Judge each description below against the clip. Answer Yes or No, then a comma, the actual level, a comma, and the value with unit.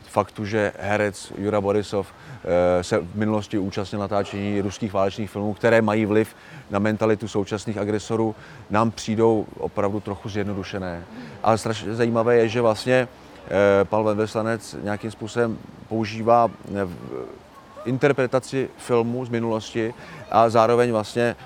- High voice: No, low, 110 Hz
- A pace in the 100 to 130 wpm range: Yes, average, 120 wpm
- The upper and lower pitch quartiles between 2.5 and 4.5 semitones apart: No, narrow, 2.1 semitones